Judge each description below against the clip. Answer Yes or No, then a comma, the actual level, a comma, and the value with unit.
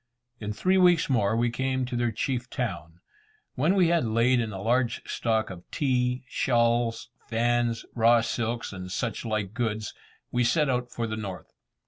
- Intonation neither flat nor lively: No, narrow, 2.3 semitones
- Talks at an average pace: Yes, average, 170 wpm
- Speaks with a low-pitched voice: Yes, low, 120 Hz